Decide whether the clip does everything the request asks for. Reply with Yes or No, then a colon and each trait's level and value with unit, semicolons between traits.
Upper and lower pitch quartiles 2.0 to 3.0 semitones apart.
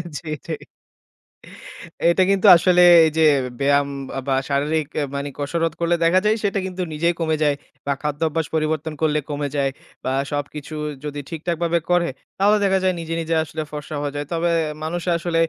Yes: average, 2.7 semitones